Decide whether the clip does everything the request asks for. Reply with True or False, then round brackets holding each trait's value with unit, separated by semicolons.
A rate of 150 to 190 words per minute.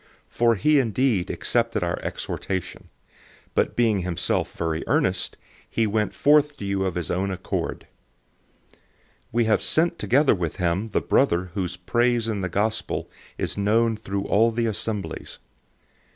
True (155 wpm)